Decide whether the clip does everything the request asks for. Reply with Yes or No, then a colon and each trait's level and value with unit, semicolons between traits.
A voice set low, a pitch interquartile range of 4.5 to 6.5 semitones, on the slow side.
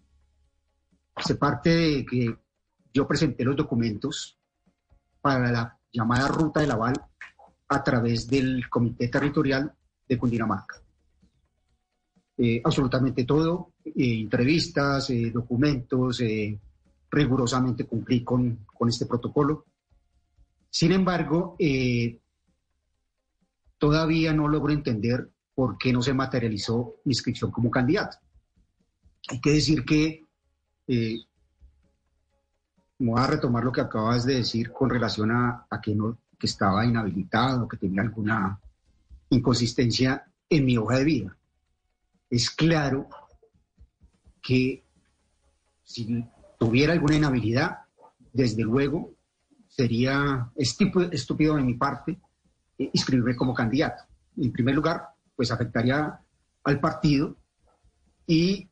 Yes: low, 125 Hz; average, 5.0 semitones; slow, 110 wpm